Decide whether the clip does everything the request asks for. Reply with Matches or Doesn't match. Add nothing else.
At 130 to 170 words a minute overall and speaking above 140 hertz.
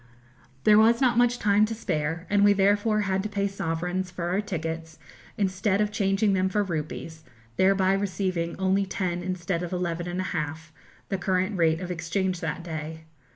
Doesn't match